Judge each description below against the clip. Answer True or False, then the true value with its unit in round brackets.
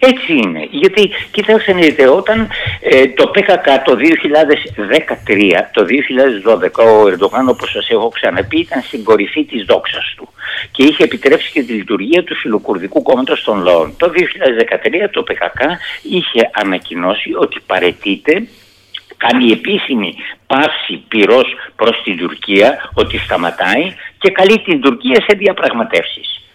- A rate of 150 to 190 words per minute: False (130 wpm)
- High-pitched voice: True (210 Hz)